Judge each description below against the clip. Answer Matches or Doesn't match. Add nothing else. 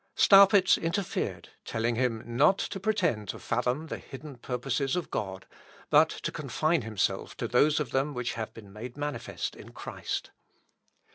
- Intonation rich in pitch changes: Matches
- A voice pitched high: Doesn't match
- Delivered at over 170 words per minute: Doesn't match